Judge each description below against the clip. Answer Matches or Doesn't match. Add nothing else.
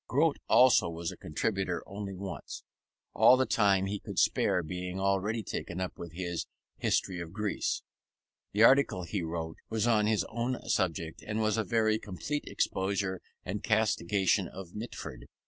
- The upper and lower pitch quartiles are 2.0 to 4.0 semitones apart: Matches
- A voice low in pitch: Matches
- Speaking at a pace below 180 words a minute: Matches